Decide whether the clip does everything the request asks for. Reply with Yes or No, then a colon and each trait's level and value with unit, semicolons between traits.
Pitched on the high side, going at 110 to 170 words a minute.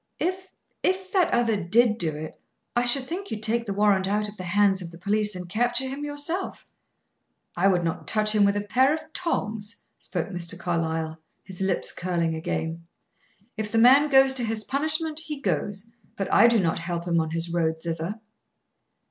No: high, 210 Hz; average, 190 wpm